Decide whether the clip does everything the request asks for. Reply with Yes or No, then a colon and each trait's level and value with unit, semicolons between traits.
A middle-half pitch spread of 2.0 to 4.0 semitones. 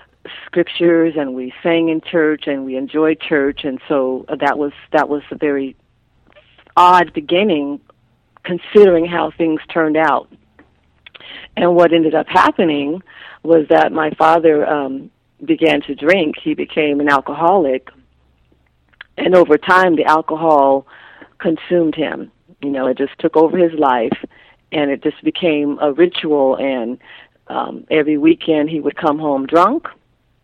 Yes: average, 2.8 semitones